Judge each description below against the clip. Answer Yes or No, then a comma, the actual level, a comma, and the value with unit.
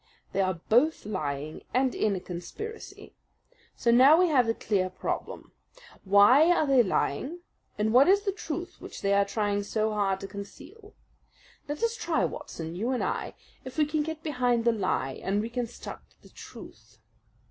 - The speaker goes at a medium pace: Yes, average, 170 wpm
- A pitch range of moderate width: No, wide, 7.3 semitones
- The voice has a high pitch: Yes, high, 235 Hz